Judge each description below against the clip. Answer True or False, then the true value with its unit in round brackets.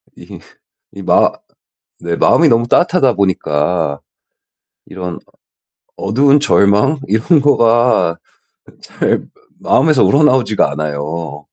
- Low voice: True (105 Hz)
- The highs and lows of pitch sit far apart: True (8.6 semitones)